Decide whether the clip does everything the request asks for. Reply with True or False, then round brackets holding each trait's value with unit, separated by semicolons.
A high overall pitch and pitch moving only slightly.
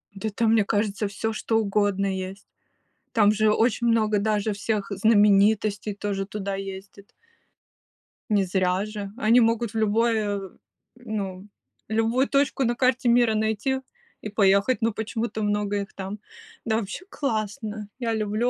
True (215 Hz; 2.1 semitones)